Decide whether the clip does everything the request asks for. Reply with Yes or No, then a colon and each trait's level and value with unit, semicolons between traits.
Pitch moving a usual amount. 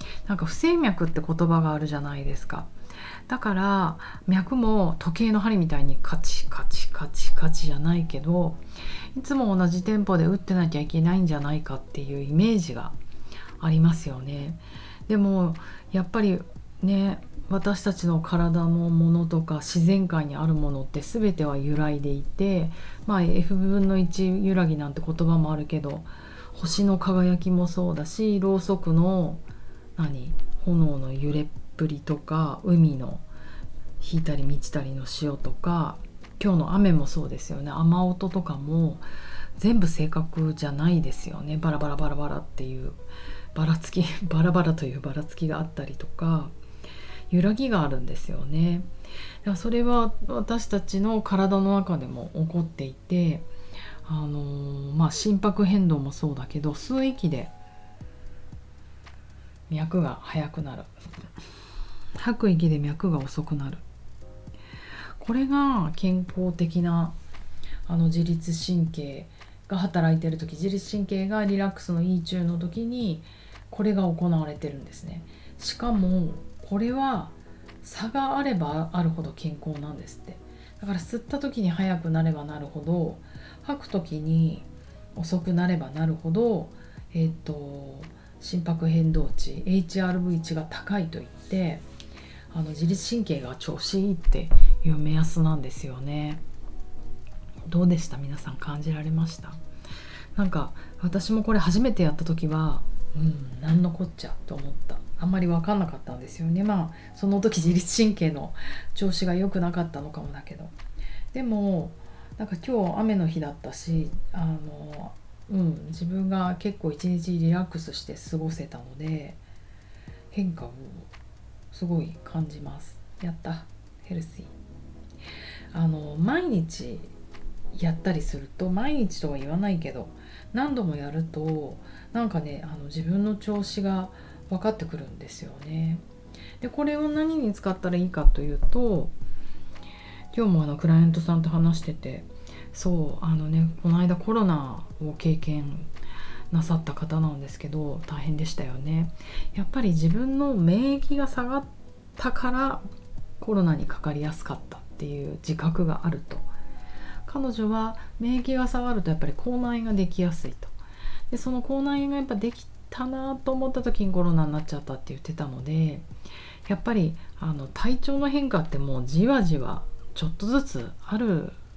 Yes: average, 4.6 semitones